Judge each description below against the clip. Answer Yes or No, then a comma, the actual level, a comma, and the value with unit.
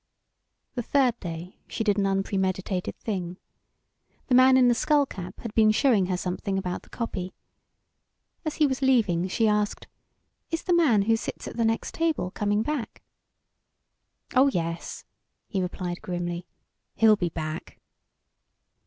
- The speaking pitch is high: Yes, high, 205 Hz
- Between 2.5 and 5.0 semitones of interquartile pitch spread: No, wide, 5.5 semitones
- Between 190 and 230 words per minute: No, average, 150 wpm